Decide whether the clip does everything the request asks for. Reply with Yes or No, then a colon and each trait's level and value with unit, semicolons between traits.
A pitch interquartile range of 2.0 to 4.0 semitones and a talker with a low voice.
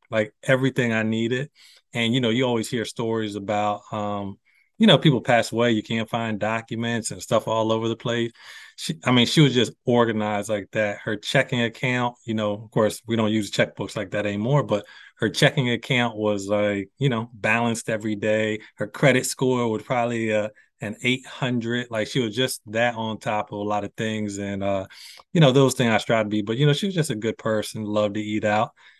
Yes: average, 2.8 semitones; low, 115 Hz